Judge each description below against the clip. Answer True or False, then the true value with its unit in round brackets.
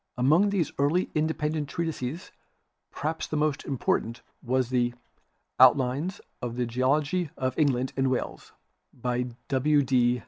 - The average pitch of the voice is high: False (135 Hz)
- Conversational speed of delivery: False (130 wpm)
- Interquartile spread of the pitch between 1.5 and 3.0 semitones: False (3.6 semitones)